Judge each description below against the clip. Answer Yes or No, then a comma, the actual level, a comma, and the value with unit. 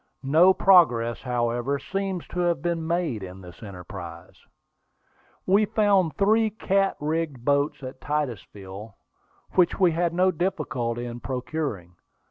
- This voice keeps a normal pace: No, slow, 125 wpm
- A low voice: No, medium, 145 Hz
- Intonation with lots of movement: Yes, wide, 7.5 semitones